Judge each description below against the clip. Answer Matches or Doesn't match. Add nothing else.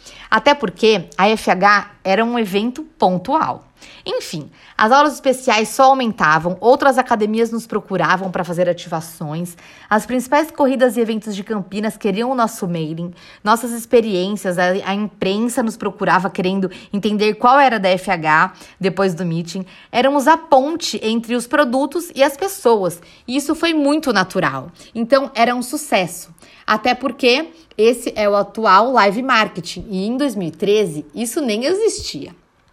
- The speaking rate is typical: Matches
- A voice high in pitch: Matches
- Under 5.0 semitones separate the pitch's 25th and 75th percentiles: Doesn't match